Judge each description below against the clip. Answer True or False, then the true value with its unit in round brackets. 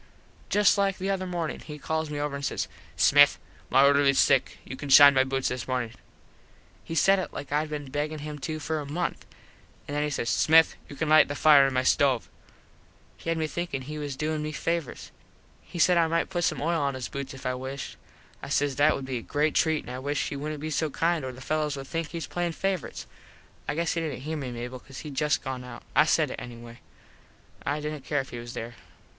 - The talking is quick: True (240 wpm)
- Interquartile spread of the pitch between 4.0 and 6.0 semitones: False (2.9 semitones)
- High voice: False (145 Hz)